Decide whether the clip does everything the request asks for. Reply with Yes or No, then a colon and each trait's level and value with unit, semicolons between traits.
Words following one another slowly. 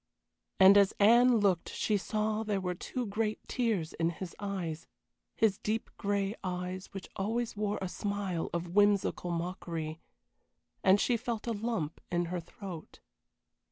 No: average, 150 wpm